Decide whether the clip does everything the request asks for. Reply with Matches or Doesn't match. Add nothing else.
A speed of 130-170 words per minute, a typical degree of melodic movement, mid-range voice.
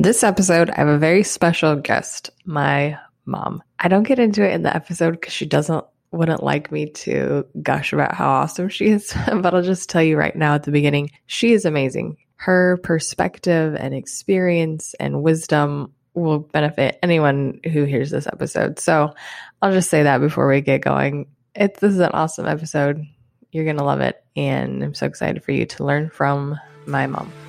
Doesn't match